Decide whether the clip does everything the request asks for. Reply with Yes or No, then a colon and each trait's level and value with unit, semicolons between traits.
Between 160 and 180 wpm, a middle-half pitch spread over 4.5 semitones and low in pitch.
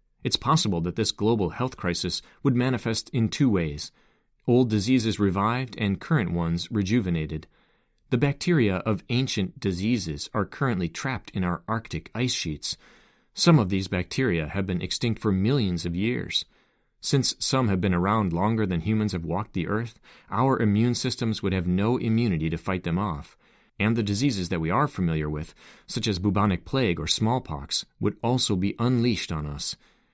Yes: average, 170 wpm; average, 5.2 semitones; low, 105 Hz